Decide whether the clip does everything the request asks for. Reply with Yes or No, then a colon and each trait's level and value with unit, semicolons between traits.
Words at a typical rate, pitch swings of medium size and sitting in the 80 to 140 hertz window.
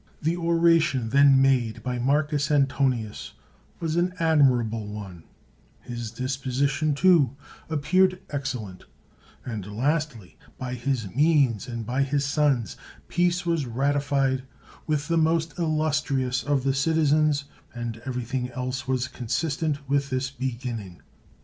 No: slow, 125 wpm; average, 3.7 semitones; low, 135 Hz